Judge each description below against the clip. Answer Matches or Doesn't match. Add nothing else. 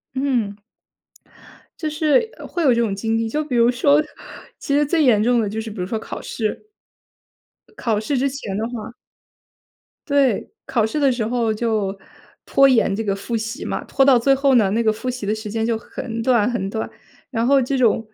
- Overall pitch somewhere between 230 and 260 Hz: Matches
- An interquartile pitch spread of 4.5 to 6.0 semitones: Doesn't match